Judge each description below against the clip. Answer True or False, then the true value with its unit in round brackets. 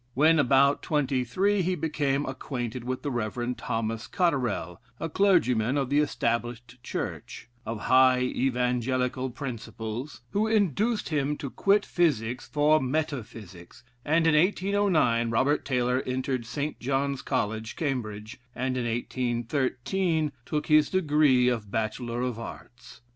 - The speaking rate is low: True (130 wpm)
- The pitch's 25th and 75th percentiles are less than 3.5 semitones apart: False (4.1 semitones)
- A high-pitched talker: False (130 Hz)